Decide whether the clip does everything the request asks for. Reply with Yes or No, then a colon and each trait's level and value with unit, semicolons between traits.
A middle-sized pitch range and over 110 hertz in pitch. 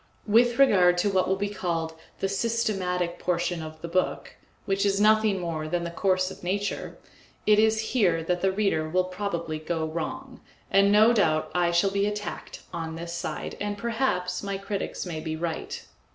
Yes: average, 3.3 semitones; medium, 185 Hz